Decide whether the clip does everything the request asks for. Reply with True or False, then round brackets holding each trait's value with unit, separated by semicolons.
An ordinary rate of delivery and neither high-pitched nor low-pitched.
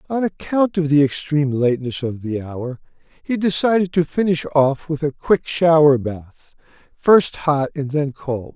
True (170 wpm; 150 Hz)